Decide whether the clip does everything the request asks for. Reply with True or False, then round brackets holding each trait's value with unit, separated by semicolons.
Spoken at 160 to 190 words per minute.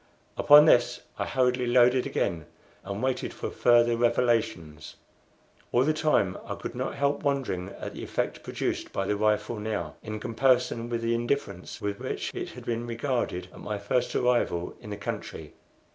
True (170 wpm)